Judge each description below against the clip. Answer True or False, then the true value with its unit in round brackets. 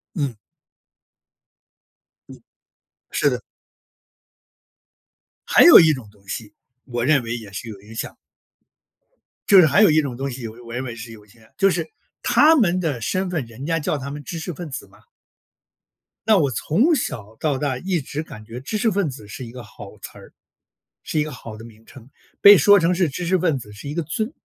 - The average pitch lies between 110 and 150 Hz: True (140 Hz)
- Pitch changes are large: True (6.8 semitones)